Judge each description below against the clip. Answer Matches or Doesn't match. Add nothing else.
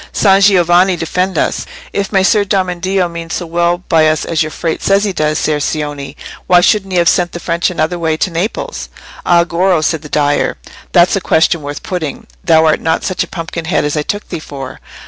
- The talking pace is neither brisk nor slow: Doesn't match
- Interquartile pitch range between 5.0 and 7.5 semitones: Doesn't match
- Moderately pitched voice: Matches